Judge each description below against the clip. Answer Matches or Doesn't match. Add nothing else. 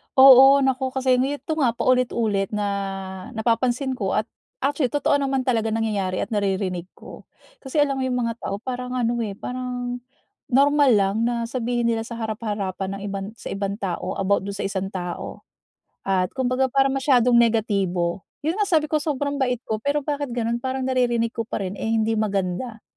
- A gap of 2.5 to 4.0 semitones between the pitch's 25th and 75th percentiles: Doesn't match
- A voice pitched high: Matches